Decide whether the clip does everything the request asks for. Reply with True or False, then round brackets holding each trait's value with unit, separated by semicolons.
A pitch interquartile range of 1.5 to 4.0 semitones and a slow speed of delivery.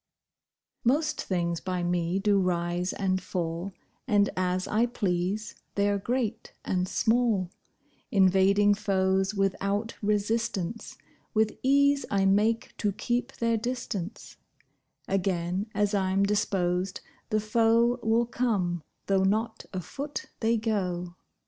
True (3.4 semitones; 115 wpm)